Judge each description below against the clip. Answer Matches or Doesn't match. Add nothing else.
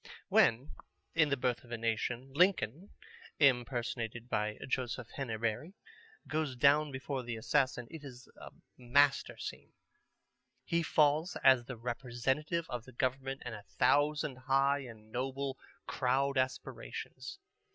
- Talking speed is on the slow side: Matches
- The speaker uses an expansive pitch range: Doesn't match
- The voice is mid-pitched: Doesn't match